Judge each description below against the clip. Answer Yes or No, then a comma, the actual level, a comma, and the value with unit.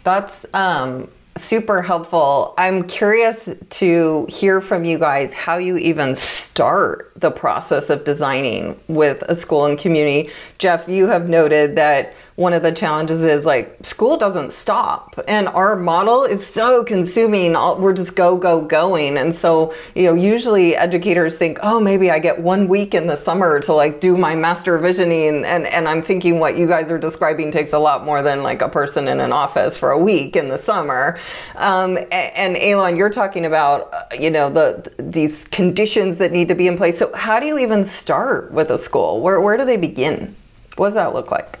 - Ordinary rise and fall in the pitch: Yes, average, 3.4 semitones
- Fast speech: No, average, 195 wpm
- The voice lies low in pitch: No, medium, 175 Hz